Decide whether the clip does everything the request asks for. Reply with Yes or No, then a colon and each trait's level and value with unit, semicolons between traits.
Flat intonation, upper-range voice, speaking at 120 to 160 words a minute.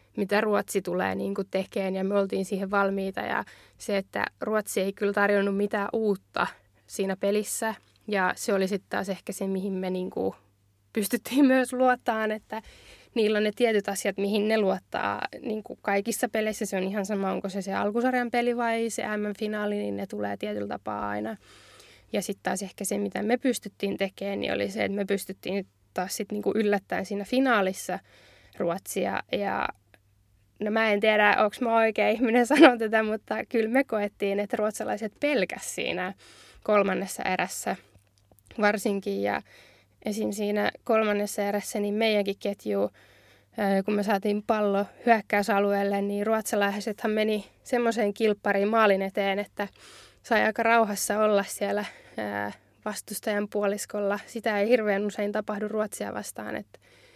Yes: narrow, 1.8 semitones; high, 205 Hz; fast, 155 wpm